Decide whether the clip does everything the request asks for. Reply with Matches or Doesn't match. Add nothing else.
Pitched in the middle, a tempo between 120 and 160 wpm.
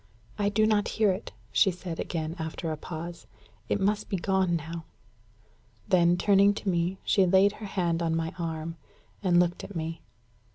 Doesn't match